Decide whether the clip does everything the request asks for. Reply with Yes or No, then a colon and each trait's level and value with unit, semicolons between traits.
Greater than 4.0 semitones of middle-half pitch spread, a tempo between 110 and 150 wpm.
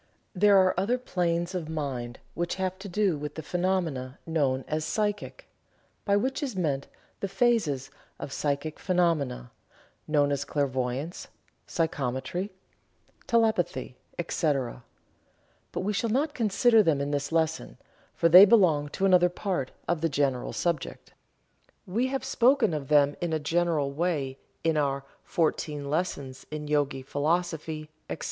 Yes: average, 4.8 semitones; average, 140 wpm